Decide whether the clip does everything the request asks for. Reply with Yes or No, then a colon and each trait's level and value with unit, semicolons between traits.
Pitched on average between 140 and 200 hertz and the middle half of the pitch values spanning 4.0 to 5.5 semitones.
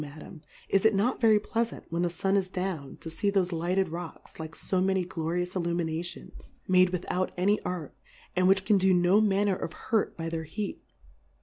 No: medium, 185 Hz; narrow, 2.5 semitones